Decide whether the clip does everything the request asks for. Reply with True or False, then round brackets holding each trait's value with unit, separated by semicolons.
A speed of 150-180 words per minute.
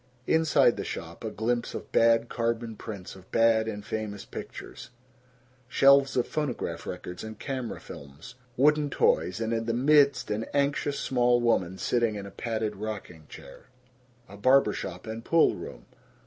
True (160 wpm)